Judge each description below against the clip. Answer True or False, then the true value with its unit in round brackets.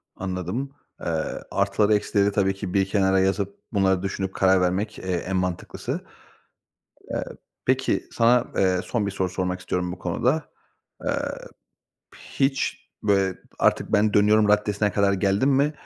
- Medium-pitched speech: False (100 Hz)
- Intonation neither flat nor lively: False (2.2 semitones)